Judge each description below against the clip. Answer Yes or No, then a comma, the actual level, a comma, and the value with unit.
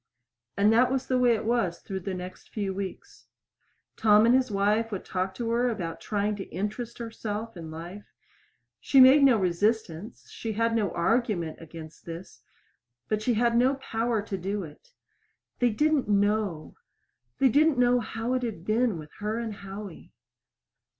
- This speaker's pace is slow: No, average, 170 wpm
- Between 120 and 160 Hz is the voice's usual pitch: No, high, 215 Hz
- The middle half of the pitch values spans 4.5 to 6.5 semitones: No, average, 3.7 semitones